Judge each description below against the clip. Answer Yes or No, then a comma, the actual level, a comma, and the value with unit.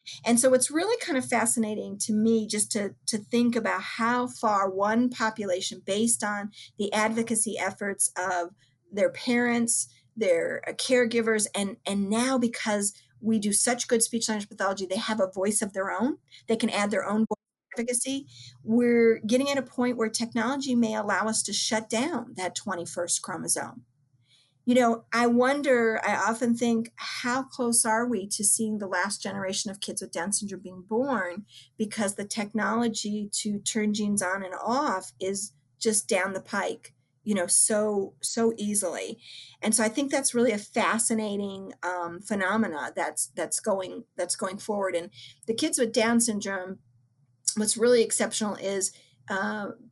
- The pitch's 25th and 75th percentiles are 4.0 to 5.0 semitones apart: No, average, 3.3 semitones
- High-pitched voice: Yes, high, 215 Hz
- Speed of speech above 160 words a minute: Yes, average, 170 wpm